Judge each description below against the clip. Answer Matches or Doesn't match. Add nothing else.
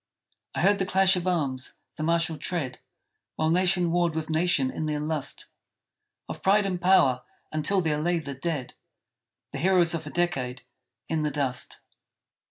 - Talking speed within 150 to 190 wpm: Matches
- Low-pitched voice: Doesn't match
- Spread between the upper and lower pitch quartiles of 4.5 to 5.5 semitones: Doesn't match